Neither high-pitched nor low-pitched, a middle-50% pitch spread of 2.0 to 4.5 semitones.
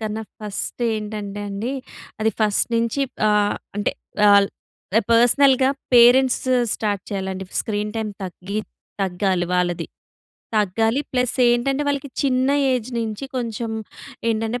No: high, 220 Hz; average, 3.3 semitones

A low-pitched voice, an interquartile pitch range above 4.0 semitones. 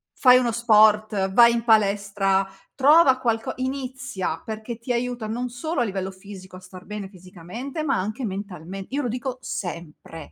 No: high, 220 Hz; average, 4.5 semitones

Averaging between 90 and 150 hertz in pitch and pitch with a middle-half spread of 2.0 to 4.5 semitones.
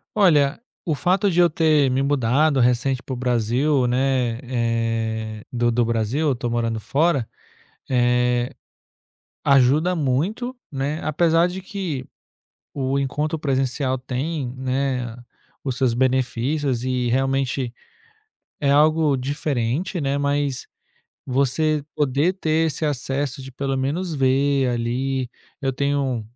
Yes: low, 135 Hz; average, 3.2 semitones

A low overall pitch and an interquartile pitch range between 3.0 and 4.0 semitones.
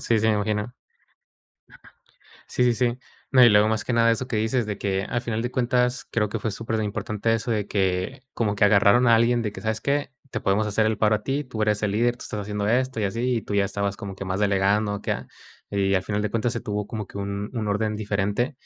No: low, 110 Hz; narrow, 2.5 semitones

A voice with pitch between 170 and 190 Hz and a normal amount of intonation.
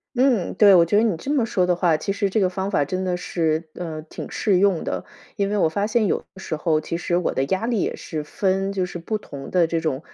Yes: medium, 185 Hz; average, 3.4 semitones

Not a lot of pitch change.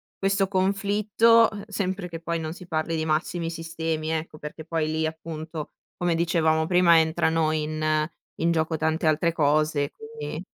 Yes: narrow, 2.3 semitones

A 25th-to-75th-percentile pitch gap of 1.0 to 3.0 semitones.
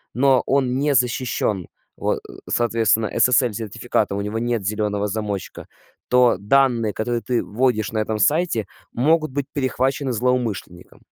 No: average, 3.4 semitones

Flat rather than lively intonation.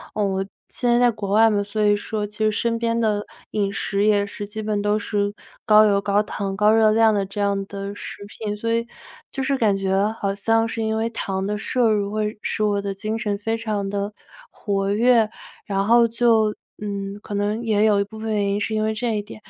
Yes: narrow, 1.6 semitones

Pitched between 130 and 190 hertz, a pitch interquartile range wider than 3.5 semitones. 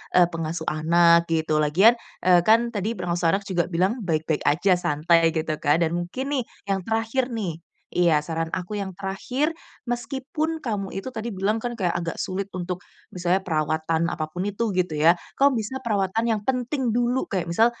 Yes: medium, 185 Hz; average, 5.2 semitones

